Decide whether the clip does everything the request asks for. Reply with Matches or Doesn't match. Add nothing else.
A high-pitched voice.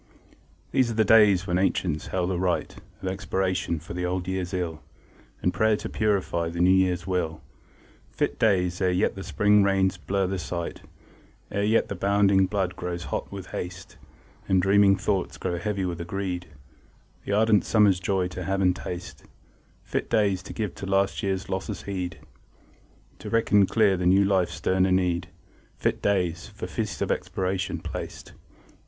Doesn't match